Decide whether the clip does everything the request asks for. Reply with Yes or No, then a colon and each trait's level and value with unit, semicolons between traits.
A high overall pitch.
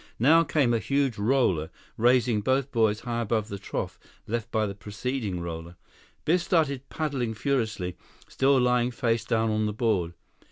No: low, 115 Hz